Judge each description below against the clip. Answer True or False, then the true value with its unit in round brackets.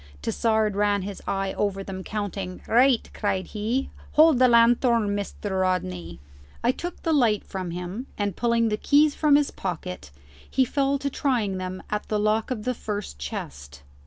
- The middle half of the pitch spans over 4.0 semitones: True (4.5 semitones)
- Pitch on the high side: True (210 Hz)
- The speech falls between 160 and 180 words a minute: True (170 wpm)